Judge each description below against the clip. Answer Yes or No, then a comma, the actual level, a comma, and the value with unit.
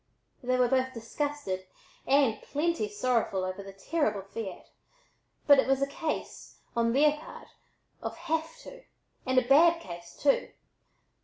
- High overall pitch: Yes, very high, 260 Hz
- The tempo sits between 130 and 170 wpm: Yes, average, 145 wpm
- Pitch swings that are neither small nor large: No, wide, 5.8 semitones